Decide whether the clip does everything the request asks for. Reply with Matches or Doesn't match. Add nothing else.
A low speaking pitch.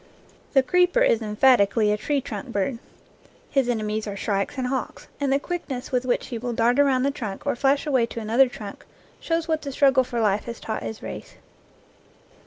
Doesn't match